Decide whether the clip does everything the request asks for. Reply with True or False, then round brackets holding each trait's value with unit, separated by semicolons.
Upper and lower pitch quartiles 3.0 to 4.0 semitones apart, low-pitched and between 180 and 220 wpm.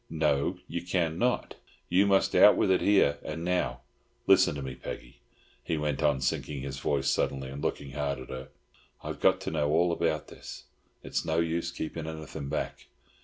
True (3.4 semitones; 75 Hz; 185 wpm)